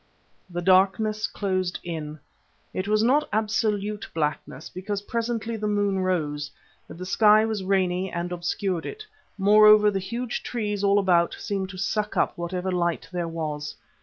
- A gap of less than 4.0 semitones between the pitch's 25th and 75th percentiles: Yes, average, 3.1 semitones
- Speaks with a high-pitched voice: Yes, high, 195 Hz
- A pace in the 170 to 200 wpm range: No, average, 155 wpm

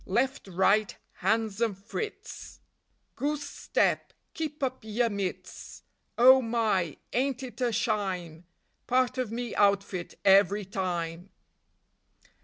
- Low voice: No, high, 215 Hz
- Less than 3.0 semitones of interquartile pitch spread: No, average, 4.8 semitones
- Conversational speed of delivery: No, slow, 110 wpm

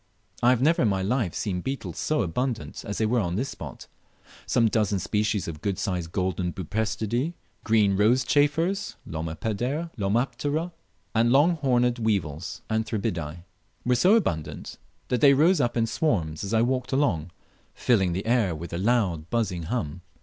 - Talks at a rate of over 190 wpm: No, average, 160 wpm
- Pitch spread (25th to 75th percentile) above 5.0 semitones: Yes, wide, 5.6 semitones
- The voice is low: Yes, low, 110 Hz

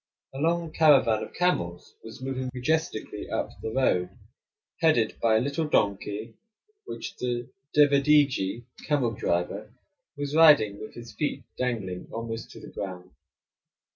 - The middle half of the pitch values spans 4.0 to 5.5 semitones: Yes, average, 5.2 semitones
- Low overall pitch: Yes, low, 120 Hz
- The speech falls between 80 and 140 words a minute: Yes, slow, 135 wpm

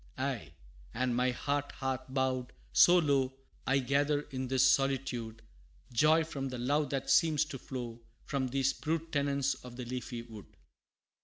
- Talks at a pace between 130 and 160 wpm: Yes, average, 155 wpm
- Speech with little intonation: Yes, narrow, 2.1 semitones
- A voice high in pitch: No, low, 135 Hz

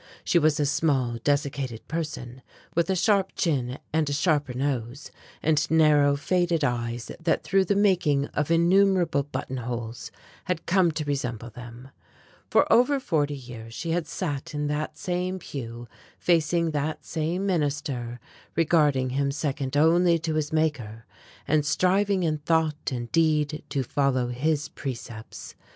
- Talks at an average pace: Yes, average, 145 wpm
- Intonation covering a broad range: No, average, 4.2 semitones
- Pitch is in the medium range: Yes, medium, 150 Hz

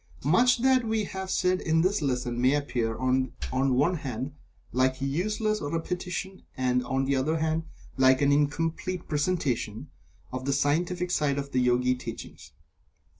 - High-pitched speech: No, medium, 145 Hz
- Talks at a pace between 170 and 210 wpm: No, average, 155 wpm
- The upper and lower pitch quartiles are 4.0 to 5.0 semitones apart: No, wide, 5.5 semitones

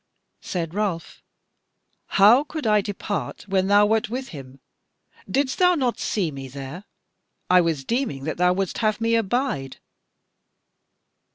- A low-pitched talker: No, high, 200 Hz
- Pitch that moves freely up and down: Yes, wide, 5.7 semitones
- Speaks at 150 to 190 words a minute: No, slow, 135 wpm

